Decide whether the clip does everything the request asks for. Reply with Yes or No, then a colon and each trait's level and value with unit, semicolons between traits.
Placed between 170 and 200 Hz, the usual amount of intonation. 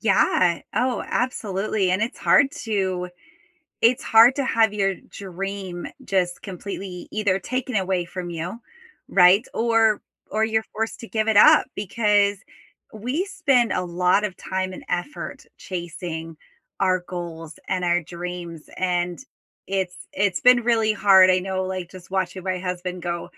Yes: high, 190 Hz; average, 3.4 semitones